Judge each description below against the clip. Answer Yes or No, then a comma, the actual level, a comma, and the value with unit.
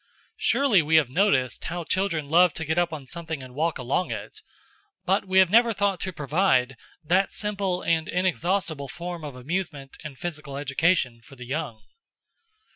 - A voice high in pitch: No, medium, 165 Hz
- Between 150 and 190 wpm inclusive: Yes, average, 170 wpm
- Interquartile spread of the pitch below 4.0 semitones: No, average, 4.8 semitones